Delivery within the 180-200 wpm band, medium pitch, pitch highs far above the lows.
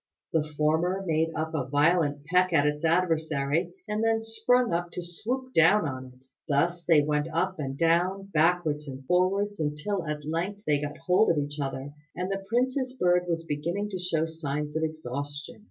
No: average, 185 wpm; medium, 165 Hz; average, 3.7 semitones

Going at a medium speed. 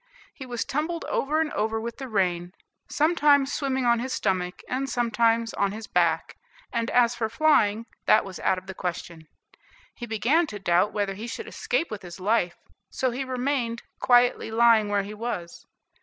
Yes: average, 180 wpm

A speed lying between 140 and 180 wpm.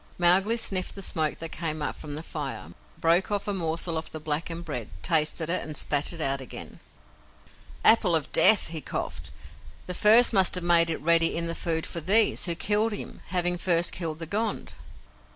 No: average, 195 wpm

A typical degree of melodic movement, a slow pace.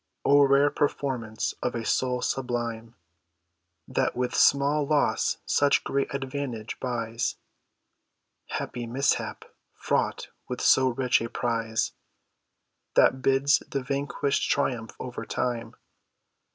Yes: average, 3.0 semitones; slow, 110 wpm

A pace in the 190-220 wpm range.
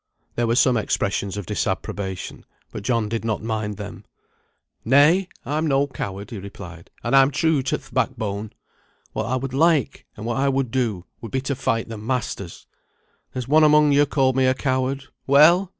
No: average, 180 wpm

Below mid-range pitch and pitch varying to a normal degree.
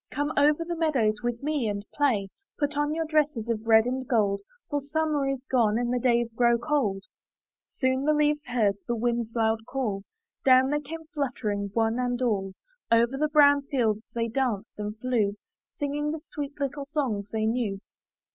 No: very high, 250 Hz; average, 4.5 semitones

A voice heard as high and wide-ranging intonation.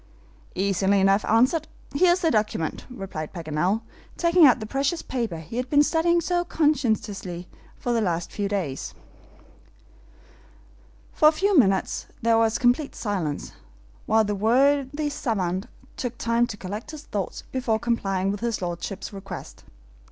Yes: high, 225 Hz; wide, 6.3 semitones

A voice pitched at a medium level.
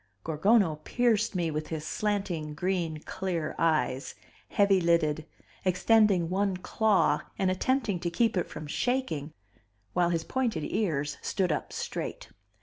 Yes: medium, 180 Hz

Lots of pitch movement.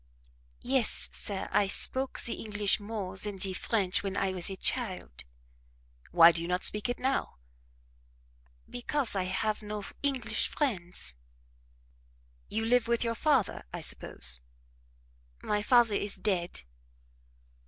No: average, 4.0 semitones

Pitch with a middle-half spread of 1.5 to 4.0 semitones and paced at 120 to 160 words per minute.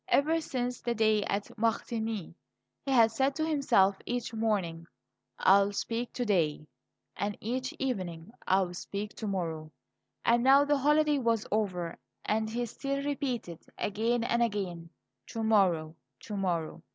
No: average, 4.4 semitones; average, 150 wpm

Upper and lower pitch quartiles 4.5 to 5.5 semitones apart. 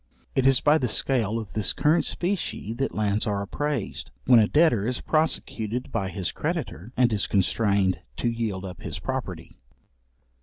Yes: average, 4.8 semitones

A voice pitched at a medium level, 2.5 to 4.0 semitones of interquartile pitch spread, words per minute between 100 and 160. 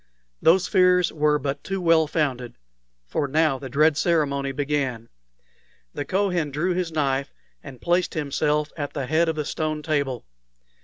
Yes: medium, 150 Hz; average, 3.0 semitones; average, 155 wpm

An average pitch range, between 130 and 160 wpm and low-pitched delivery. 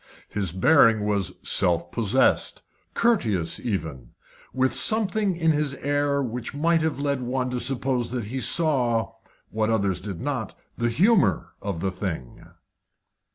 No: wide, 6.0 semitones; average, 145 wpm; low, 125 Hz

